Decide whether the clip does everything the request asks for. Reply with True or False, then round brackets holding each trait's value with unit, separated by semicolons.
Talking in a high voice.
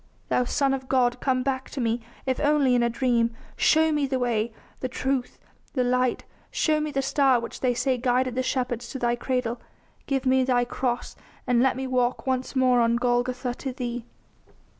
True (255 Hz)